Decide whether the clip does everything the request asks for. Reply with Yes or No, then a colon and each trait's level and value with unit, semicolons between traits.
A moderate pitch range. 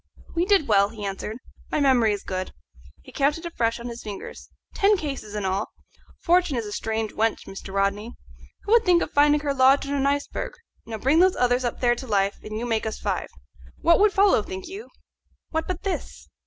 No: wide, 7.1 semitones